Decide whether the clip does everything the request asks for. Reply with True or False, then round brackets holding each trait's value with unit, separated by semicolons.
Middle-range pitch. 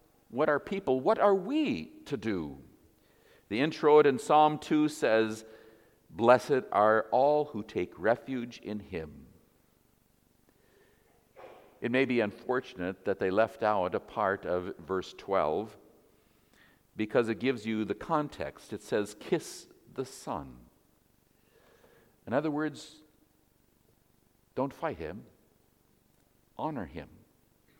False (125 Hz)